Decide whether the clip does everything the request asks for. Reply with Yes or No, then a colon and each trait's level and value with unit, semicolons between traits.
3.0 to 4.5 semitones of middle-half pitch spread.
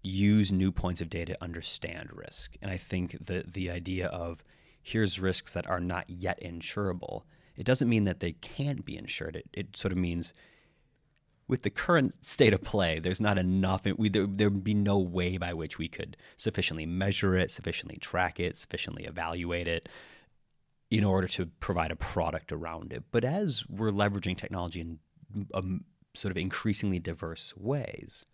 Yes: average, 3.3 semitones